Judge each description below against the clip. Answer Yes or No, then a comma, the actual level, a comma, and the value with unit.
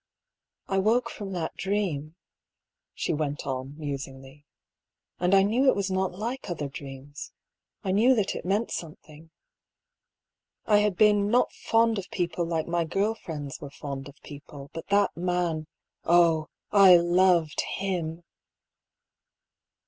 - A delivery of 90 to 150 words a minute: Yes, average, 145 wpm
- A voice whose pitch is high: No, medium, 175 Hz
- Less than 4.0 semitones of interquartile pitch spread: No, average, 5.0 semitones